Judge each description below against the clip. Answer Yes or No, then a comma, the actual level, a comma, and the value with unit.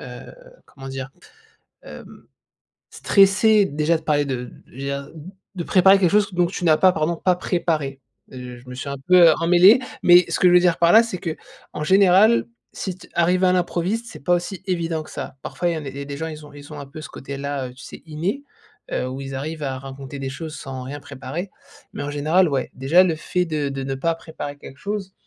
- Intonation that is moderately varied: Yes, average, 4.6 semitones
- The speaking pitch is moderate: Yes, medium, 160 Hz